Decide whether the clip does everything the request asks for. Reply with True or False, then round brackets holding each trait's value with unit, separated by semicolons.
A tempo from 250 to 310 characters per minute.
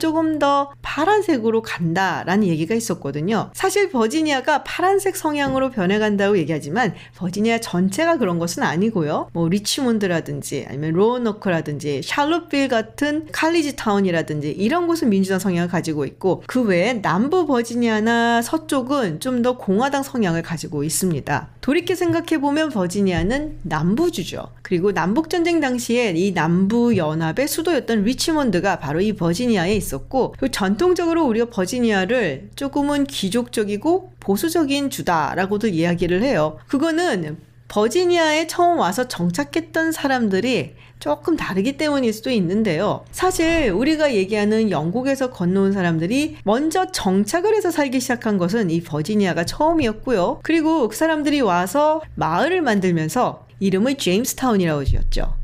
False (365 characters per minute)